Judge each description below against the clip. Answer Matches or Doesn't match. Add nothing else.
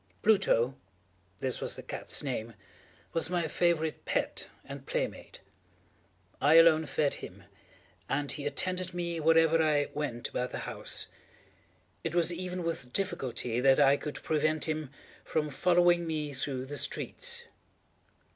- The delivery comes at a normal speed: Doesn't match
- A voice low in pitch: Doesn't match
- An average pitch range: Matches